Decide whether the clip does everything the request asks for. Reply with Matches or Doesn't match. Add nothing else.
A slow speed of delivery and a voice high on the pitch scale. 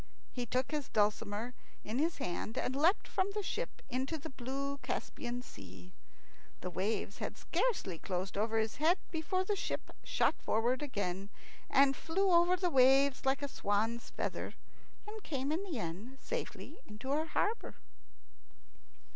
Doesn't match